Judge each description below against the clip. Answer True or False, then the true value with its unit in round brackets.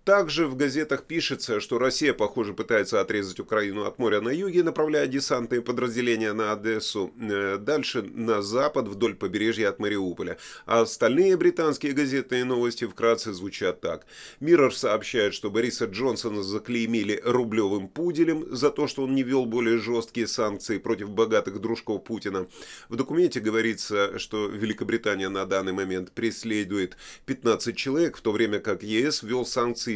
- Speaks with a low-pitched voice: True (115 Hz)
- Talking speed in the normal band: True (145 wpm)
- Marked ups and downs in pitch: False (4.4 semitones)